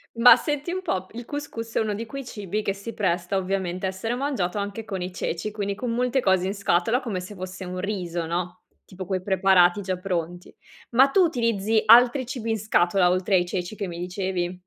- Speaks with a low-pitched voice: No, high, 195 Hz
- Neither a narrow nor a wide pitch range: Yes, average, 3.9 semitones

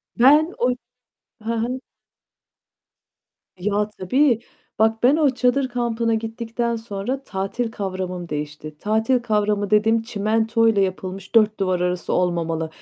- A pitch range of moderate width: Yes, average, 3.7 semitones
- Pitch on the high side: Yes, high, 220 Hz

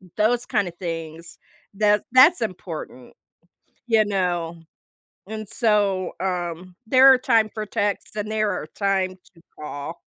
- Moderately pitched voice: No, high, 195 Hz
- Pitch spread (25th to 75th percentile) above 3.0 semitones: Yes, average, 3.8 semitones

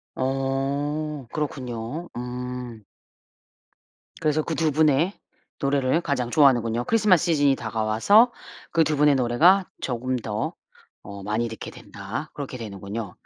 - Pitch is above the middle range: No, low, 135 Hz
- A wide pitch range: No, average, 4.6 semitones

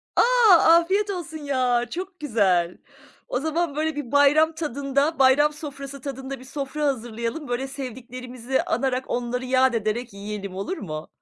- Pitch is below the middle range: No, very high, 265 Hz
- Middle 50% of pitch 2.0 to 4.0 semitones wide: Yes, average, 3.7 semitones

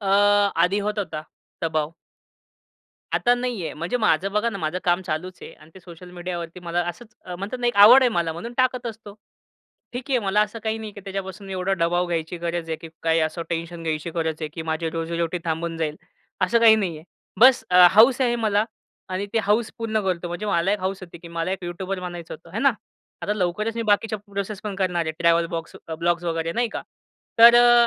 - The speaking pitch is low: No, medium, 185 Hz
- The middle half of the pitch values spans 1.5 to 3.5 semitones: No, average, 4.2 semitones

